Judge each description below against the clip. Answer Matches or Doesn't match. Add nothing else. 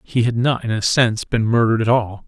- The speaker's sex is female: Doesn't match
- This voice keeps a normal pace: Doesn't match